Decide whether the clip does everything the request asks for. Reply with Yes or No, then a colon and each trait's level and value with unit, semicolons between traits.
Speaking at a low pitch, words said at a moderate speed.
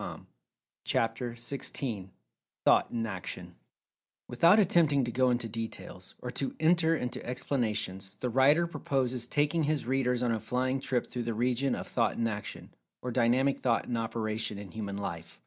Yes: low, 120 Hz; average, 165 wpm